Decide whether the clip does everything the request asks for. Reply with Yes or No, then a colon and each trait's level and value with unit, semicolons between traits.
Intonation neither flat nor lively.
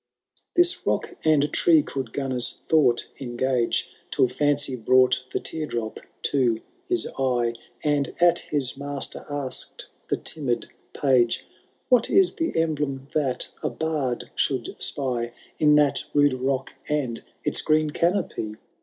Yes: average, 3.2 semitones